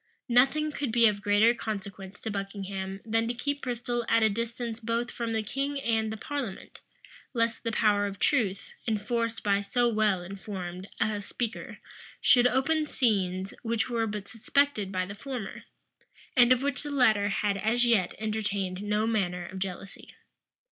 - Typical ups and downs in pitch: Yes, average, 3.2 semitones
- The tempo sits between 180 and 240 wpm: No, average, 165 wpm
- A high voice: Yes, high, 220 Hz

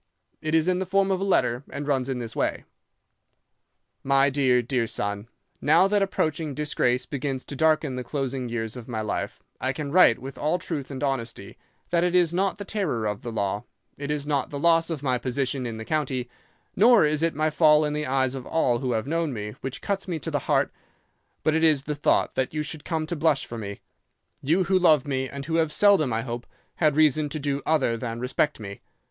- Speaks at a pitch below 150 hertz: Yes, medium, 140 Hz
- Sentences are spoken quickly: Yes, fast, 220 wpm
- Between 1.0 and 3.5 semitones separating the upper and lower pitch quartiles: No, average, 4.1 semitones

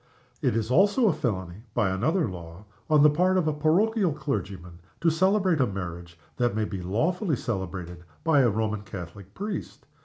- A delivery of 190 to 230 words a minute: No, average, 165 wpm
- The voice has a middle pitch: No, low, 115 Hz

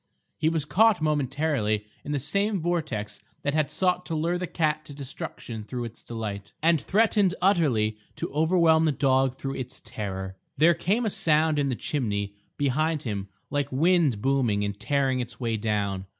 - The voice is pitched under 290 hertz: Yes, medium, 140 Hz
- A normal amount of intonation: No, wide, 6.3 semitones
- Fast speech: No, average, 175 wpm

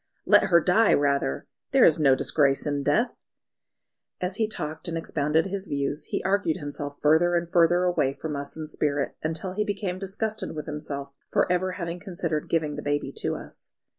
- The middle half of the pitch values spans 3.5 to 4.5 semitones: Yes, average, 3.8 semitones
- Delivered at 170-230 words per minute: Yes, average, 185 wpm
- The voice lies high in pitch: No, medium, 160 Hz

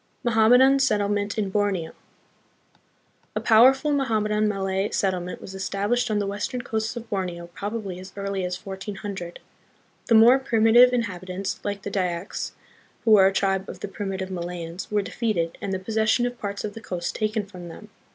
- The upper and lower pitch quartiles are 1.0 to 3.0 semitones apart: Yes, average, 2.7 semitones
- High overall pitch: Yes, high, 205 Hz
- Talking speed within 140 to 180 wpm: Yes, average, 165 wpm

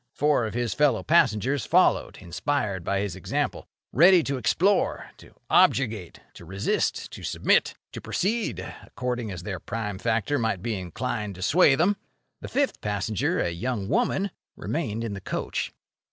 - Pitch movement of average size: No, wide, 6.6 semitones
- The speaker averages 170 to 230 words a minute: No, average, 155 wpm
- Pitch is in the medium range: No, low, 115 Hz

